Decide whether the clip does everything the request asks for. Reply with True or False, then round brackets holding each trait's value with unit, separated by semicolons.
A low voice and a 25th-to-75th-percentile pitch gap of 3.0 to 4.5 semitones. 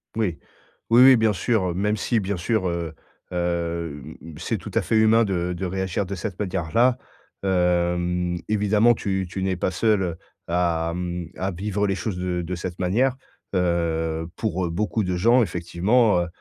True (90 Hz; 3.4 semitones)